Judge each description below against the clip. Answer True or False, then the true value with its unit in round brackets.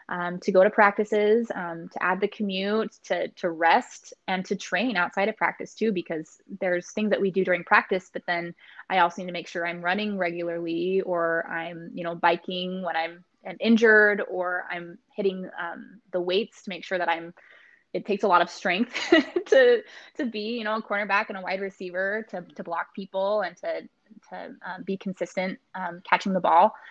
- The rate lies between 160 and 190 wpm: False (200 wpm)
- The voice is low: False (190 Hz)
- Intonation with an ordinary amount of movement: True (3.2 semitones)